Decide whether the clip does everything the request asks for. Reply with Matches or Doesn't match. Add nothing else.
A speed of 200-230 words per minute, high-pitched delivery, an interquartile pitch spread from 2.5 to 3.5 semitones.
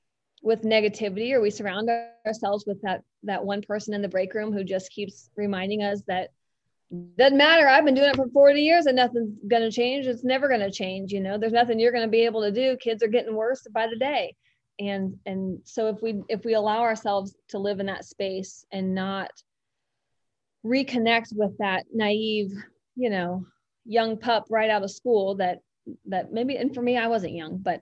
Matches